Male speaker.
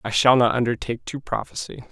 Yes: male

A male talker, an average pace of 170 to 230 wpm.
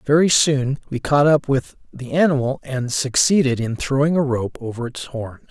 Yes: male; average, 185 wpm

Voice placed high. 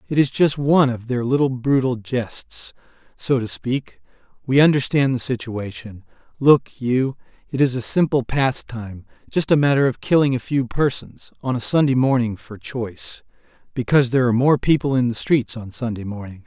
No: low, 125 Hz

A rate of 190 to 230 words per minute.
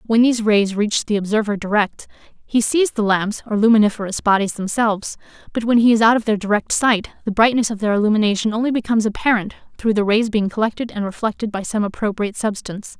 Yes: average, 200 wpm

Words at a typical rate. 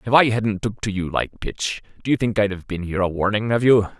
No: fast, 285 wpm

